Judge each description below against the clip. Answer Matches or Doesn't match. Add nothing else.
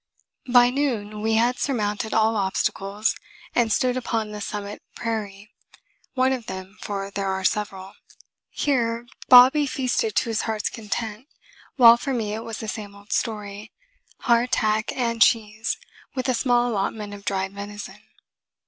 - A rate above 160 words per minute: Doesn't match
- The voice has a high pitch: Matches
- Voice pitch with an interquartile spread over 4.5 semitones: Doesn't match